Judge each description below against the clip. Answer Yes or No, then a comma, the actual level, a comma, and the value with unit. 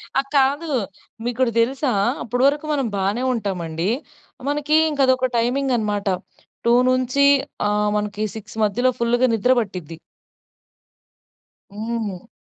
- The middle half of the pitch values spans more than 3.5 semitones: Yes, average, 4.0 semitones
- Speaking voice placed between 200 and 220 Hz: No, high, 235 Hz